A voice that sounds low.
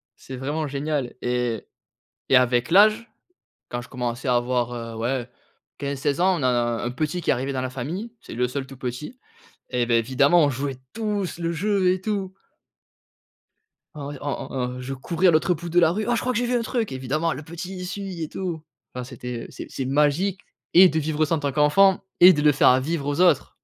No: medium, 150 Hz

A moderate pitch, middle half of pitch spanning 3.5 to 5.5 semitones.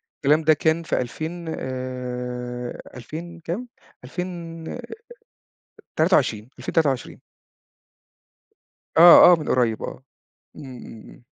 Yes: medium, 145 Hz; average, 5.0 semitones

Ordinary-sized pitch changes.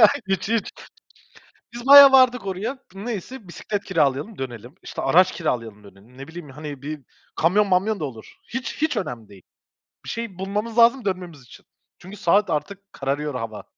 No: wide, 7.8 semitones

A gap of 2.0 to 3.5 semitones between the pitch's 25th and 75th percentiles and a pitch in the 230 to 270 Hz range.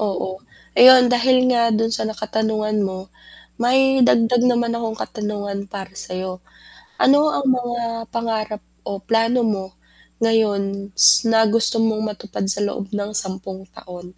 No: average, 2.9 semitones; high, 220 Hz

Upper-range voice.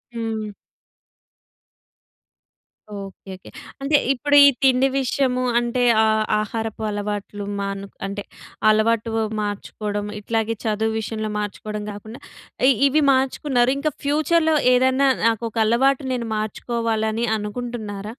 Yes: high, 225 Hz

